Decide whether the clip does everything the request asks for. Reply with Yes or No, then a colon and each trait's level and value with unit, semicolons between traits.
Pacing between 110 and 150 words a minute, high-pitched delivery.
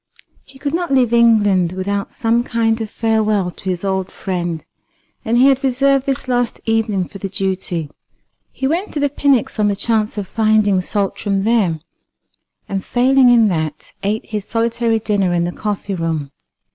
No: average, 170 wpm; high, 215 Hz